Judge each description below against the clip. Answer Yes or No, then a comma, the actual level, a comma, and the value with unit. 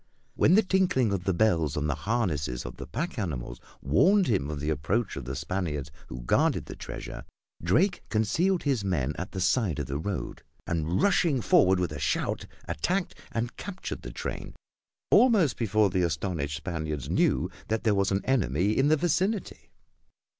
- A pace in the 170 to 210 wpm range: Yes, average, 175 wpm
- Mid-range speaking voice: No, very low, 95 Hz